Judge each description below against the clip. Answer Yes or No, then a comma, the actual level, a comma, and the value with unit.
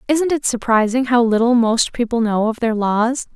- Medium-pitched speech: No, high, 235 Hz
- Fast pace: No, average, 195 wpm